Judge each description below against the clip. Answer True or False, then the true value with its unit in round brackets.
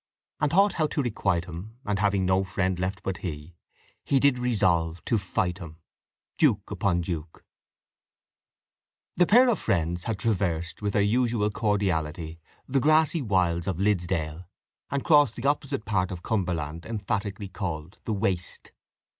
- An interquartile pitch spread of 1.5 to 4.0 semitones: False (4.6 semitones)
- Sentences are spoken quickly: False (150 wpm)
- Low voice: True (95 Hz)